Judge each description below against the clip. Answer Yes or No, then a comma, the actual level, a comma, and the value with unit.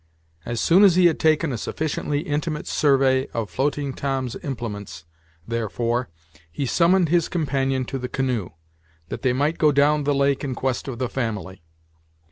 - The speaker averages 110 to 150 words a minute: No, average, 165 wpm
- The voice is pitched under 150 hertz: Yes, low, 135 Hz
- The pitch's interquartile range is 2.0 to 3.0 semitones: No, average, 3.5 semitones